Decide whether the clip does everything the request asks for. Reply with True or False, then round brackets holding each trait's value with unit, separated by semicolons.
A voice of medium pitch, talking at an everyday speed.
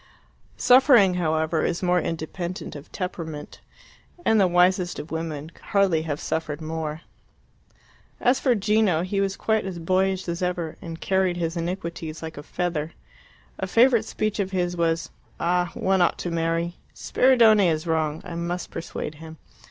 True (175 Hz; 160 wpm)